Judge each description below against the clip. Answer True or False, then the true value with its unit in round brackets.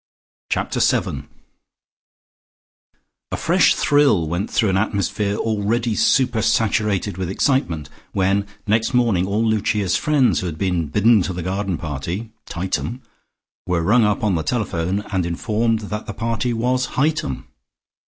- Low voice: True (105 Hz)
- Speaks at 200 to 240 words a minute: False (140 wpm)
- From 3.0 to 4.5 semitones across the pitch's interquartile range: True (3.9 semitones)